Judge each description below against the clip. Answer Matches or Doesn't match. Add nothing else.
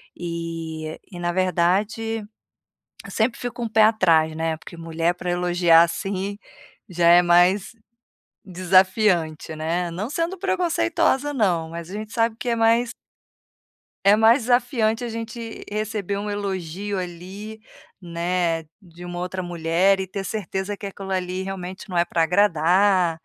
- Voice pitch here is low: Doesn't match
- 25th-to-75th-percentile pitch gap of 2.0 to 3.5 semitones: Doesn't match